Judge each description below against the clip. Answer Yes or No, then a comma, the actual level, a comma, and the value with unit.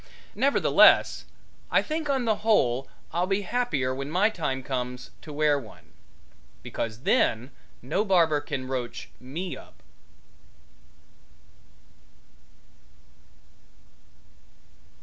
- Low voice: No, medium, 150 Hz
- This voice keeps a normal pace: No, slow, 95 wpm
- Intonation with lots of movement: Yes, wide, 7.8 semitones